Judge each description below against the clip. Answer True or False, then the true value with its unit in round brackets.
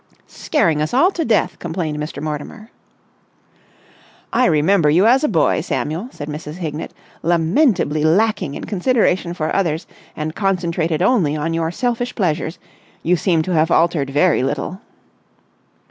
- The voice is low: False (170 Hz)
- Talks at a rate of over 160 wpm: False (145 wpm)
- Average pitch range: True (4.3 semitones)